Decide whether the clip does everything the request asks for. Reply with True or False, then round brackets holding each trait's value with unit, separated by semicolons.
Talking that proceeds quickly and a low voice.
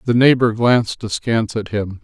False (175 wpm; 115 Hz)